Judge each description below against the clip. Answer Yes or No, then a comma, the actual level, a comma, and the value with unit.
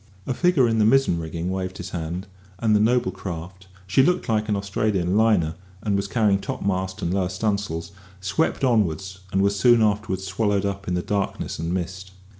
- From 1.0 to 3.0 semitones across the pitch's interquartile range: Yes, narrow, 2.6 semitones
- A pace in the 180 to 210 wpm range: Yes, average, 190 wpm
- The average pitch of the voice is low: Yes, low, 100 Hz